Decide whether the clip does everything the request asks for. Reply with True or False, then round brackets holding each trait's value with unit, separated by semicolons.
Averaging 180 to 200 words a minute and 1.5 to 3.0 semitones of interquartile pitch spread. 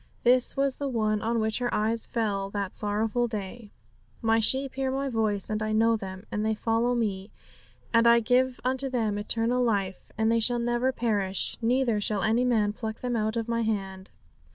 True (195 wpm; 2.4 semitones)